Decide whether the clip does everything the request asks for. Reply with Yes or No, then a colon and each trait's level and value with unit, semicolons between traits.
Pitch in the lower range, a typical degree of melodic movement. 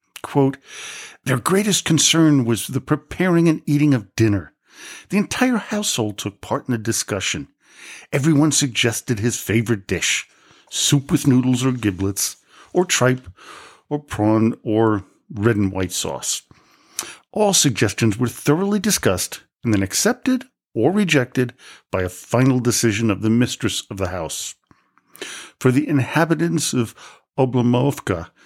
No: low, 125 Hz; wide, 5.9 semitones